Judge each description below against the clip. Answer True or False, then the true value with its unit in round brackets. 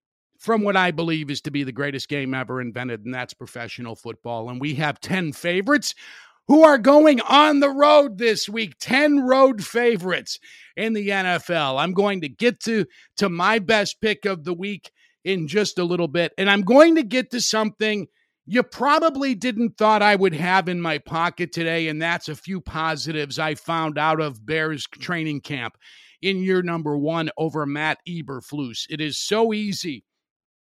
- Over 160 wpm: True (180 wpm)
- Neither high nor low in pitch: True (175 Hz)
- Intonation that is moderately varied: False (6.2 semitones)